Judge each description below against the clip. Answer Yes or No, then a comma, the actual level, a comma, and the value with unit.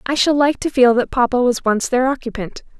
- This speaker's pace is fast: Yes, fast, 235 wpm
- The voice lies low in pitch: No, very high, 255 Hz